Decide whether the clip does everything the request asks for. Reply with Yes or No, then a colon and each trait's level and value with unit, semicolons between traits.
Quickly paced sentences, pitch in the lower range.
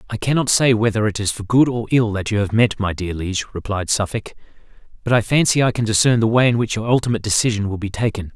Yes: fast, 250 wpm; low, 110 Hz